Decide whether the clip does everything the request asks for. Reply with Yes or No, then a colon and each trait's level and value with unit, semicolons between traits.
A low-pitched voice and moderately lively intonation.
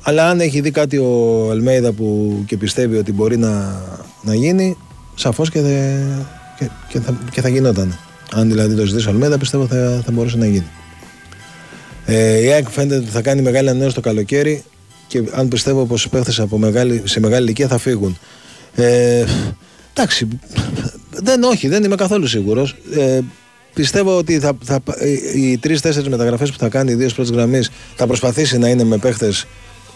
Yes: low, 125 Hz; average, 3.8 semitones